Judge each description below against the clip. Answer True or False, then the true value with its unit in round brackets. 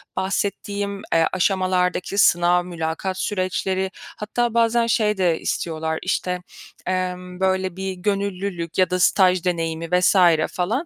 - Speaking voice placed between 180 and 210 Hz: True (185 Hz)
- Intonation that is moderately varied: False (1.9 semitones)